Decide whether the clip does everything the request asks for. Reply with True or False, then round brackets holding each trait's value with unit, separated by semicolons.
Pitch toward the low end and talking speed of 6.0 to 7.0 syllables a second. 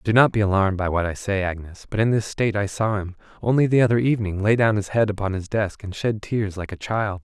True (105 Hz; 6.2 syllables/s)